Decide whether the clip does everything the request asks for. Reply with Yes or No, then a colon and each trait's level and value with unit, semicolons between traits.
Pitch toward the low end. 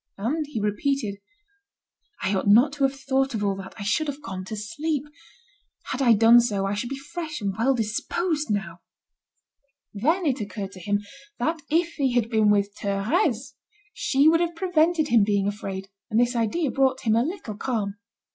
No: high, 240 Hz